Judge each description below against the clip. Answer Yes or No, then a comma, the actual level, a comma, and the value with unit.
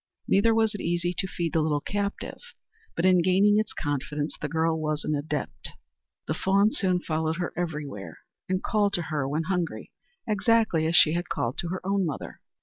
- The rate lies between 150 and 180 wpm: No, average, 190 wpm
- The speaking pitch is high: No, medium, 175 Hz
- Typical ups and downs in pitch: Yes, average, 4.2 semitones